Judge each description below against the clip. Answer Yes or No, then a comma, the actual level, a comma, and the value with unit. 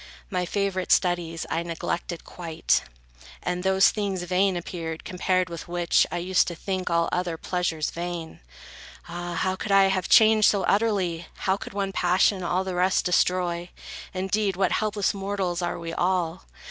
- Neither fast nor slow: Yes, average, 160 wpm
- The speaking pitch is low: No, medium, 180 Hz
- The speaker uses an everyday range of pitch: No, narrow, 1.9 semitones